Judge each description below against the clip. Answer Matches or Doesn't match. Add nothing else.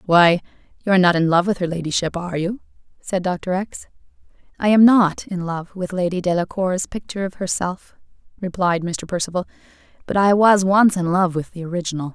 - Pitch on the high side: Doesn't match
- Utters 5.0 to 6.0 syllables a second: Matches